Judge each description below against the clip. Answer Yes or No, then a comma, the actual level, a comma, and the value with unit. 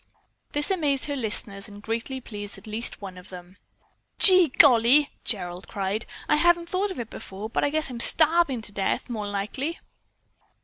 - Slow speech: No, average, 175 wpm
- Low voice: No, high, 235 Hz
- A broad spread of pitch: Yes, wide, 6.4 semitones